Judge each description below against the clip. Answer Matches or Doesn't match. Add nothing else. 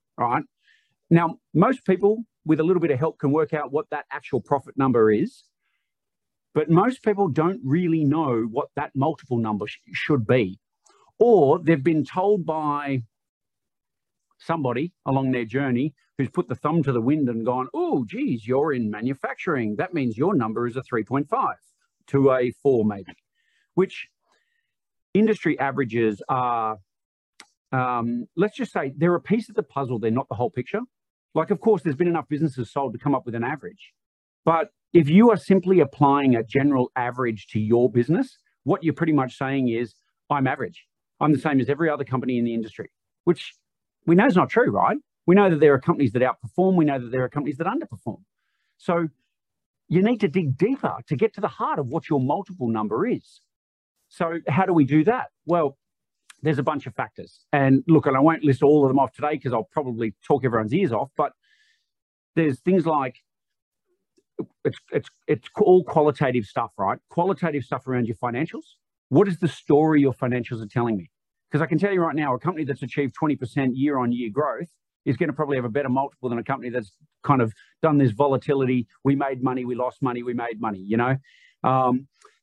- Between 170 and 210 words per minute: Matches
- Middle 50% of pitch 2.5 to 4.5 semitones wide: Doesn't match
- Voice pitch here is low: Doesn't match